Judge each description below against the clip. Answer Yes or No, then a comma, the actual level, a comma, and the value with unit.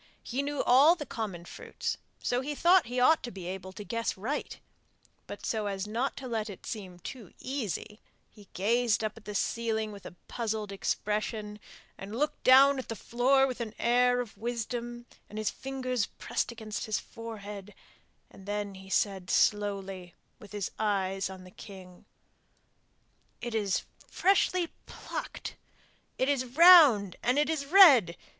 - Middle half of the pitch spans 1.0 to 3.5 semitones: No, average, 4.0 semitones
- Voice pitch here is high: Yes, high, 220 Hz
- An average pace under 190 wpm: Yes, average, 165 wpm